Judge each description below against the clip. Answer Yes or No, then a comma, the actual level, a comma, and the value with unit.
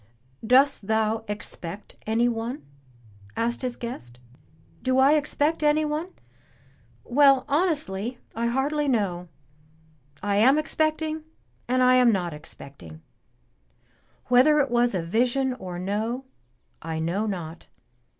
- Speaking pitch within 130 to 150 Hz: No, high, 240 Hz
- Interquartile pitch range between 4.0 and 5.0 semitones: No, wide, 5.6 semitones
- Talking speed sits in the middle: No, slow, 110 wpm